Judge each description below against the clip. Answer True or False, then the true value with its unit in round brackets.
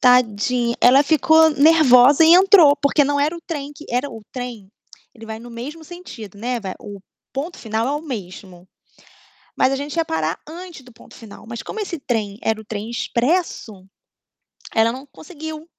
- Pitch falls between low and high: False (255 Hz)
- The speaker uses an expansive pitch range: True (5.8 semitones)